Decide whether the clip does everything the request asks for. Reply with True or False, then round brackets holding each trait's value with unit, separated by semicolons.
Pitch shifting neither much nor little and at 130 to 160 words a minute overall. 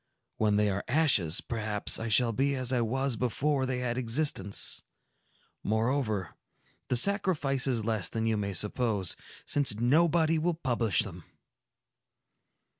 True (4.4 semitones; 135 wpm)